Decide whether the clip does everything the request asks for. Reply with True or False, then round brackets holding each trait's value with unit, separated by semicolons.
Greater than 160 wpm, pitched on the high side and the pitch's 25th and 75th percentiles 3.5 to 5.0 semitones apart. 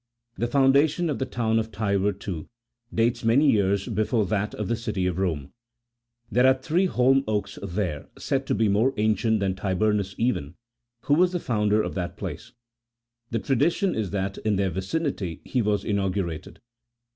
False (175 wpm; 105 Hz; 4.2 semitones)